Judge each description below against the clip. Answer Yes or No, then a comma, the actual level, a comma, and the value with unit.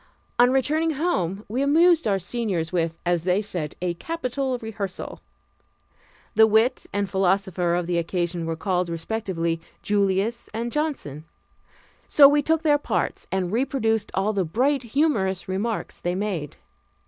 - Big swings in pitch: Yes, wide, 6.2 semitones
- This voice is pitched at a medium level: No, high, 205 Hz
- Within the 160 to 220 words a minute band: No, average, 145 wpm